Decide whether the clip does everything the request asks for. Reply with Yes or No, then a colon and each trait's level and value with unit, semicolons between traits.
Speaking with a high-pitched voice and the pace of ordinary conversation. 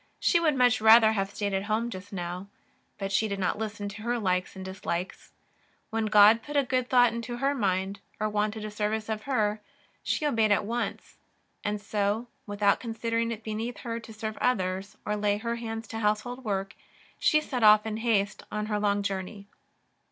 Yes: high, 215 Hz; average, 190 wpm